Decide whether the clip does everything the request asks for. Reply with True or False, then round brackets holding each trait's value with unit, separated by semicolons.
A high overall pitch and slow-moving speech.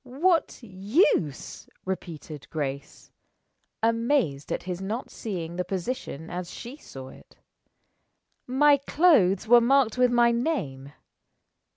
True (215 Hz; 110 wpm)